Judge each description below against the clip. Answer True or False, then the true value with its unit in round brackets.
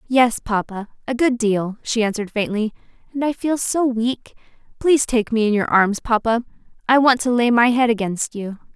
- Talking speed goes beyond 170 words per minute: True (190 wpm)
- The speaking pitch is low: False (230 Hz)